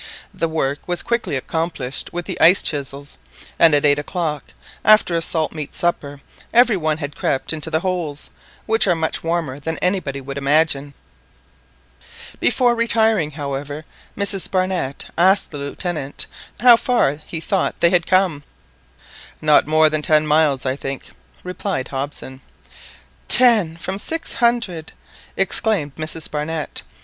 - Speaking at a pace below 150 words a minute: Yes, average, 140 wpm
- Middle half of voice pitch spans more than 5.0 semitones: No, average, 4.3 semitones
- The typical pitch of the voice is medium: Yes, medium, 160 Hz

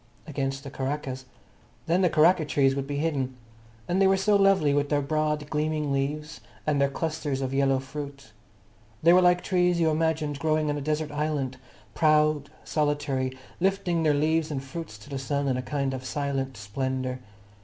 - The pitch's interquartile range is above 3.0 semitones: No, narrow, 2.5 semitones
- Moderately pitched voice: Yes, medium, 145 Hz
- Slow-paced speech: No, average, 180 wpm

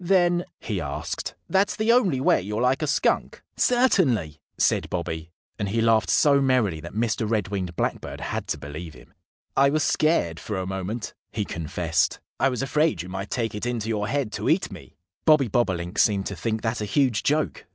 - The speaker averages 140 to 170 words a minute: No, average, 195 wpm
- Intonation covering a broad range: Yes, wide, 7.0 semitones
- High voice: No, low, 110 Hz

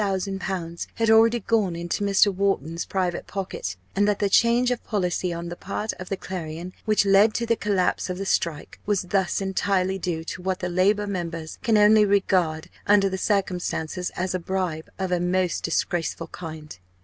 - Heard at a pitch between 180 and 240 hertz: Yes, high, 190 Hz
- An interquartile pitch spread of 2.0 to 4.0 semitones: Yes, average, 2.7 semitones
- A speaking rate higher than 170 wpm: Yes, average, 185 wpm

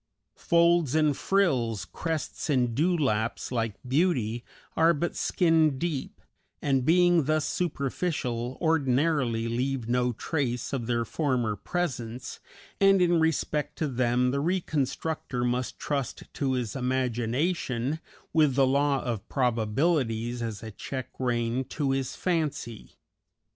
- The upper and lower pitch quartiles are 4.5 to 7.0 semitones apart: Yes, average, 4.8 semitones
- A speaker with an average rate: No, slow, 120 wpm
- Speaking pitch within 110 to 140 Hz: Yes, low, 135 Hz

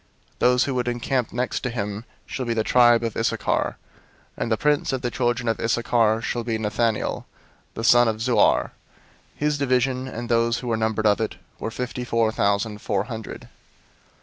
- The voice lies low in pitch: Yes, low, 115 Hz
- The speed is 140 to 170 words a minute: No, average, 185 wpm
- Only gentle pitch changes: Yes, narrow, 2.0 semitones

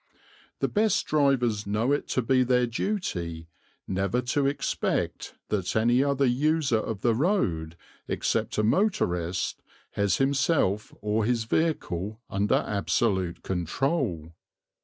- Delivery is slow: Yes, slow, 120 wpm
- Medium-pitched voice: No, low, 115 Hz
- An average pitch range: No, wide, 6.2 semitones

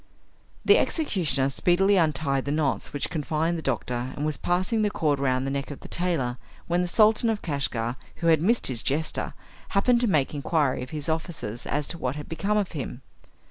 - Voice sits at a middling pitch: Yes, medium, 155 Hz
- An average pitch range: Yes, average, 4.5 semitones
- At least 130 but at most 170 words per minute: No, average, 200 wpm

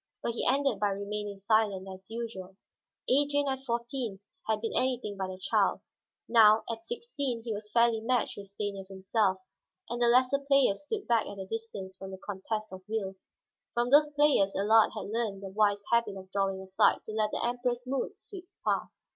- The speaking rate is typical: Yes, average, 190 wpm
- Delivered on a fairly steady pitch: No, average, 3.9 semitones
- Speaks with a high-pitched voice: Yes, high, 220 Hz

